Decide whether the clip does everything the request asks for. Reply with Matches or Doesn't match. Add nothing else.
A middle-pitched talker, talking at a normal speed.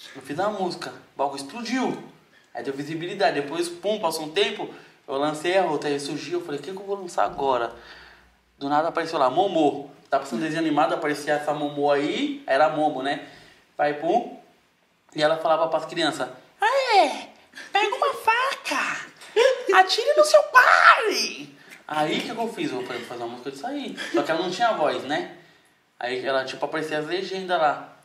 Doesn't match